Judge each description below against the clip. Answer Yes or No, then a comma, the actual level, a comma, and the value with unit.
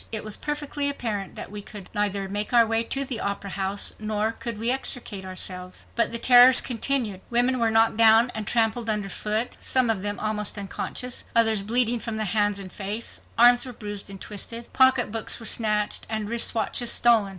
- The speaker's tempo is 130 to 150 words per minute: No, average, 195 wpm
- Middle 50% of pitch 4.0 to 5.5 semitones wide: No, narrow, 2.5 semitones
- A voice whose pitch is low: No, high, 220 Hz